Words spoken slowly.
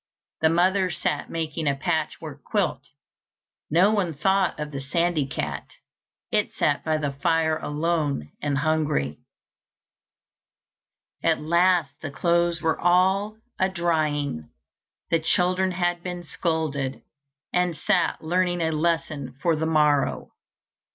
Yes: slow, 125 wpm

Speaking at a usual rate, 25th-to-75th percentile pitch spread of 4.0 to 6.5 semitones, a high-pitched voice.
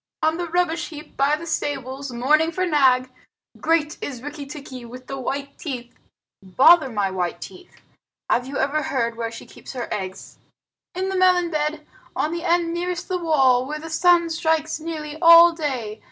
Yes: average, 180 wpm; average, 4.5 semitones; very high, 300 Hz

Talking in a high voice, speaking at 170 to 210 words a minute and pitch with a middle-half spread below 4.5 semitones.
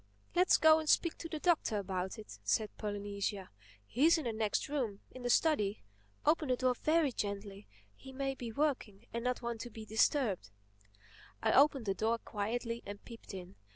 No: high, 230 Hz; average, 175 wpm; average, 5.1 semitones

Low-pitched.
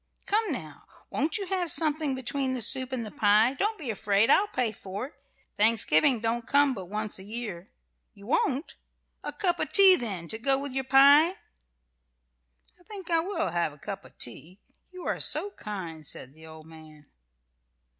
No: high, 240 Hz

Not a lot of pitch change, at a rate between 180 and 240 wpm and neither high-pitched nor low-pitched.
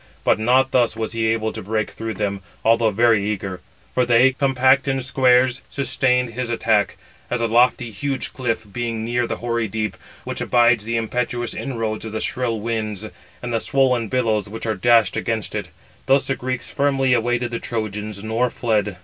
No: narrow, 2.3 semitones; average, 185 wpm; low, 115 Hz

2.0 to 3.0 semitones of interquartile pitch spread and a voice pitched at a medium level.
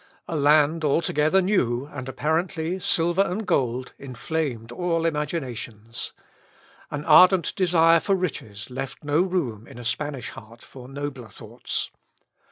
No: average, 5.1 semitones; medium, 150 Hz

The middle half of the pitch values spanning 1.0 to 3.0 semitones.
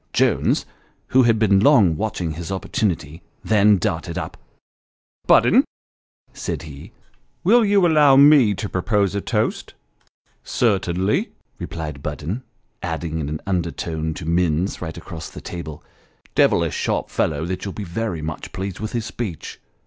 No: average, 5.1 semitones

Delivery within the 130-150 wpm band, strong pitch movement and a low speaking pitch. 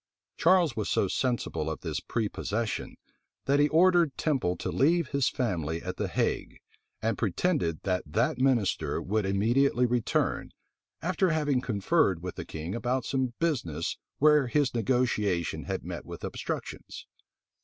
Yes: average, 145 wpm; wide, 6.8 semitones; low, 120 Hz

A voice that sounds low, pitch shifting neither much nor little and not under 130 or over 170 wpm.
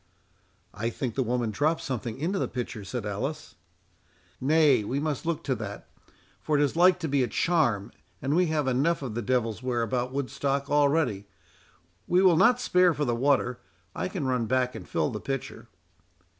No: low, 130 Hz; average, 4.8 semitones; average, 180 wpm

